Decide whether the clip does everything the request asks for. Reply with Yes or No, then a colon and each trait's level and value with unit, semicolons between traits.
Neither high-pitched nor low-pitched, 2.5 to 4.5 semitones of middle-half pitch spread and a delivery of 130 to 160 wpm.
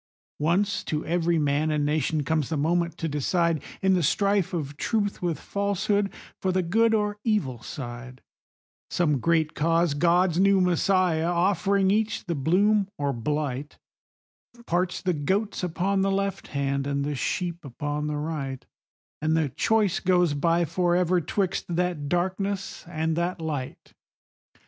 Yes: medium, 170 Hz; average, 4.1 semitones; average, 150 wpm